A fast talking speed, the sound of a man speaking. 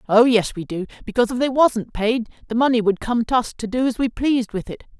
No: fast, 265 wpm; female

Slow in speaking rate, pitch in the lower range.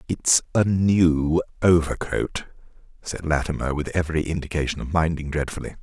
Yes: slow, 125 wpm; very low, 80 Hz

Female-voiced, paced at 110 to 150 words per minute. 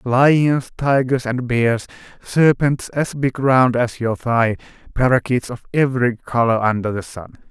No: male; average, 145 wpm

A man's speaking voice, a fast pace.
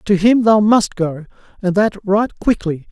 No: male; average, 185 wpm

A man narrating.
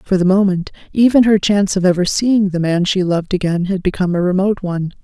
No: female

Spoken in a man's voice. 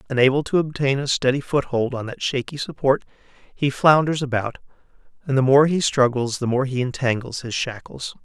Yes: male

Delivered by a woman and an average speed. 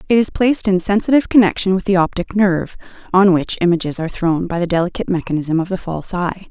No: female; fast, 210 wpm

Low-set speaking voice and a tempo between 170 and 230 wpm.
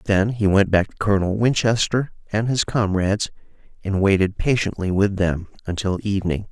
No: low, 100 Hz; average, 155 wpm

